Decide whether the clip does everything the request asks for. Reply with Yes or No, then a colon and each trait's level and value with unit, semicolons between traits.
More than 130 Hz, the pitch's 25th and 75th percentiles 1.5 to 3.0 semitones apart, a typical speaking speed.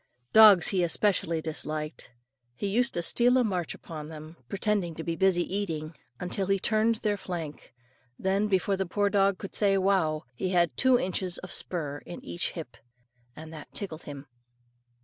No: medium, 185 Hz; average, 3.8 semitones; average, 170 wpm